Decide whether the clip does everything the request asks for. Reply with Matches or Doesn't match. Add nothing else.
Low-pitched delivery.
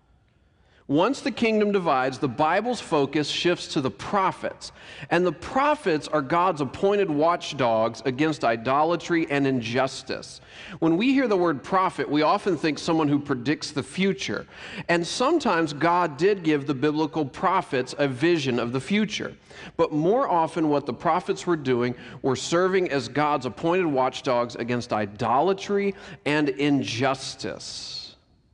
Doesn't match